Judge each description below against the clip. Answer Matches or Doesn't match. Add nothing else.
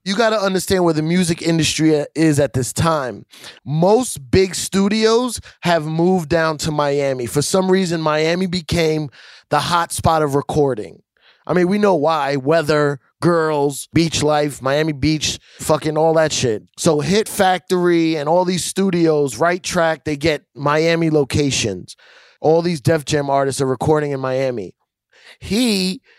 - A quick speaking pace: Doesn't match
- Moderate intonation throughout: Matches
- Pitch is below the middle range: Doesn't match